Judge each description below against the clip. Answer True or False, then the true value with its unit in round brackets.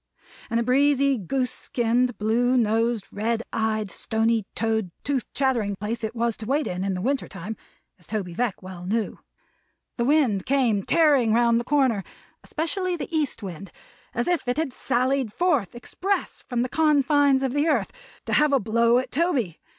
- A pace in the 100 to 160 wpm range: False (175 wpm)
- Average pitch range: True (4.2 semitones)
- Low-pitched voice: False (240 Hz)